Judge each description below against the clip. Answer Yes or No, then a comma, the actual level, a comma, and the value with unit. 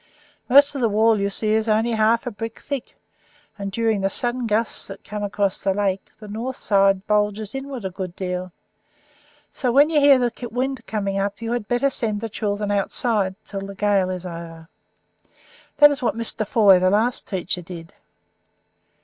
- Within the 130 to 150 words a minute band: No, average, 185 wpm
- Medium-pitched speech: No, high, 210 Hz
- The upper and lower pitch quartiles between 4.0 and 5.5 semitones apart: No, average, 3.2 semitones